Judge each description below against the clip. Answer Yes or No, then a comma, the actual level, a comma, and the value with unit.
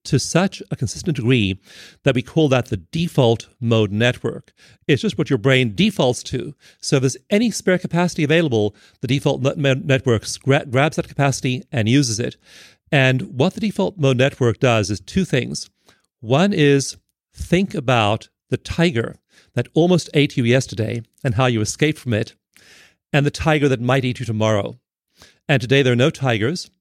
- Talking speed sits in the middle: Yes, average, 170 wpm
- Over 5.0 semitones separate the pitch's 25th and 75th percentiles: No, average, 4.7 semitones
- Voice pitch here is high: No, low, 135 Hz